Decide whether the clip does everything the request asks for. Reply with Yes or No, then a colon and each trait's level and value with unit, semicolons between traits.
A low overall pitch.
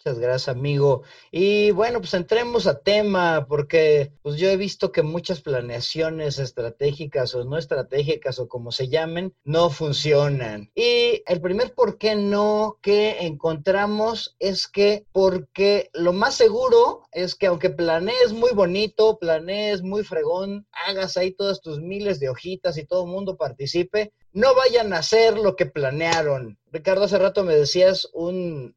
No: medium, 185 Hz